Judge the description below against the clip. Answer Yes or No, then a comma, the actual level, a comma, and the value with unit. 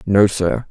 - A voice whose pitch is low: Yes, low, 100 Hz